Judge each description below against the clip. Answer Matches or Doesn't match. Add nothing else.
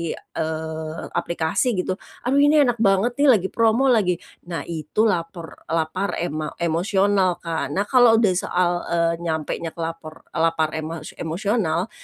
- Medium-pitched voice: Matches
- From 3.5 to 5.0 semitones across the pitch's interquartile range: Matches